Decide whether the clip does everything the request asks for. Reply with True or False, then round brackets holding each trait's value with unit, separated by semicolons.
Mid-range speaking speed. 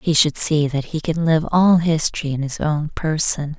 False (215 wpm)